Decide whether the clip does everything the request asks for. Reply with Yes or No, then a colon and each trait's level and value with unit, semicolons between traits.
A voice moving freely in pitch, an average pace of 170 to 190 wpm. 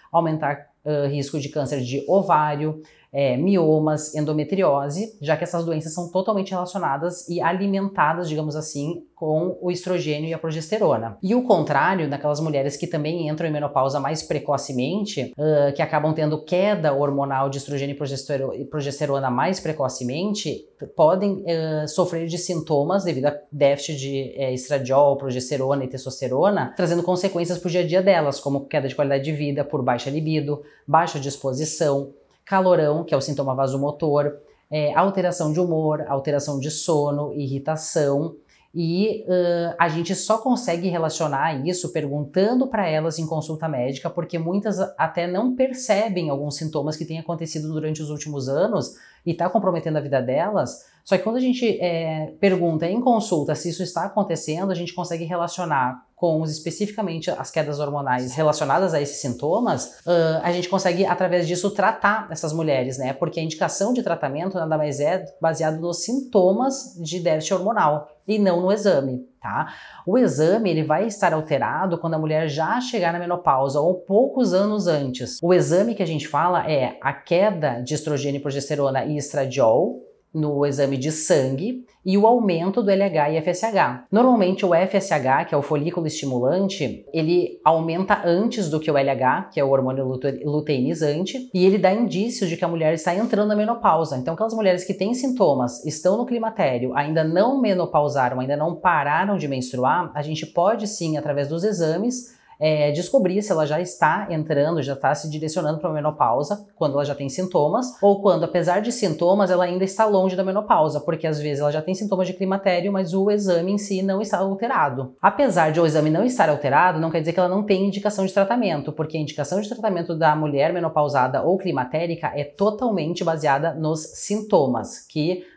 No: average, 4.2 semitones; average, 175 wpm